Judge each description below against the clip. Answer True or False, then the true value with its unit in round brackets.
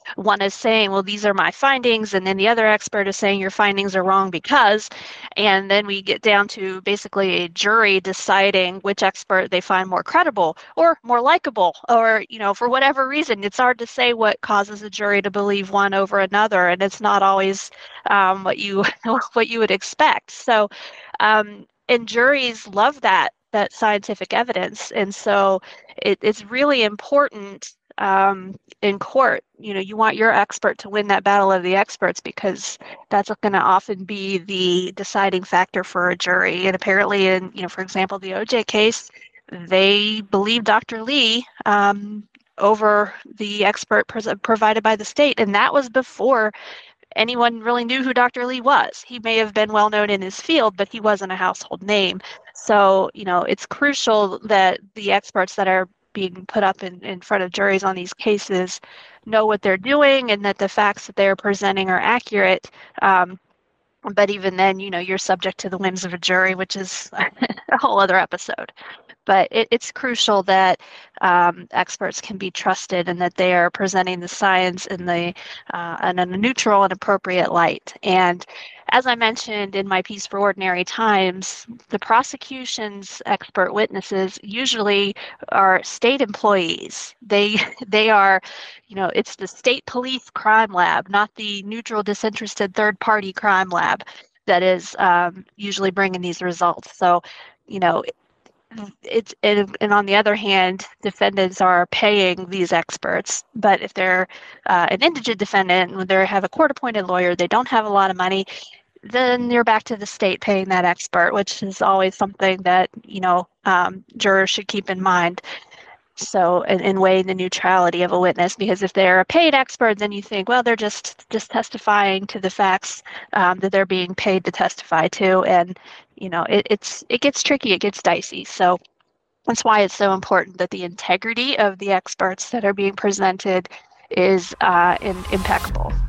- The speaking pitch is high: True (200 Hz)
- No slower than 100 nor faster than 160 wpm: False (180 wpm)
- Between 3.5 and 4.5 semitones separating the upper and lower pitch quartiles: False (2.6 semitones)